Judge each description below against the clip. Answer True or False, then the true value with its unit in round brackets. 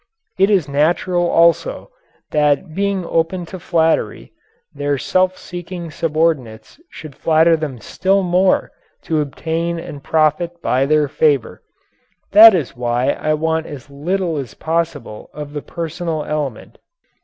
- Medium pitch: True (160 Hz)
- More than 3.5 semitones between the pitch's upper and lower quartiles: False (3.1 semitones)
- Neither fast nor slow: False (130 wpm)